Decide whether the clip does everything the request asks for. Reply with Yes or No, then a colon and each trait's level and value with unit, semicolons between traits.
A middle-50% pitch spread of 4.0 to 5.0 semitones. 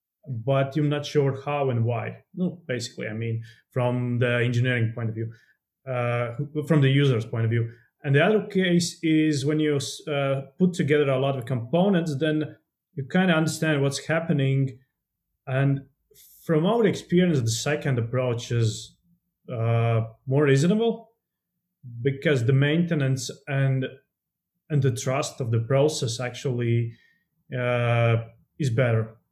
Yes: average, 4.4 semitones